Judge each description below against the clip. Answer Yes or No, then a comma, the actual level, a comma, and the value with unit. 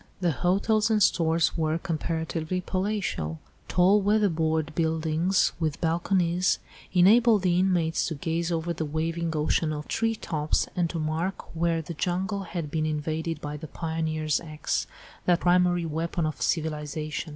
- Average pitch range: No, narrow, 2.3 semitones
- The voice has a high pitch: No, medium, 165 Hz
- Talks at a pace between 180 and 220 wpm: No, average, 145 wpm